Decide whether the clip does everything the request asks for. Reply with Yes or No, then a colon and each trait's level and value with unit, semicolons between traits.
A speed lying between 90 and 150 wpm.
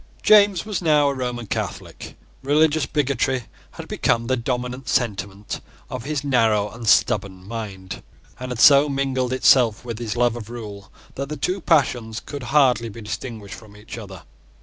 No: average, 165 wpm